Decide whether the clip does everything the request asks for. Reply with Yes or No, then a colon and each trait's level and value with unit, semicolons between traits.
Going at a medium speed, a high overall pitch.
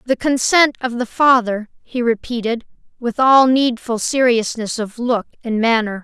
Yes: average, 150 wpm; high, 240 Hz